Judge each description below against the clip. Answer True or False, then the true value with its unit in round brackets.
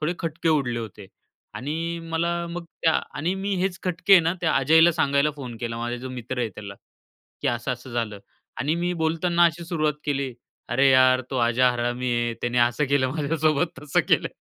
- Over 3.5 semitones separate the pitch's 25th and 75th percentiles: True (5.2 semitones)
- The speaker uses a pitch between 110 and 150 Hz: True (145 Hz)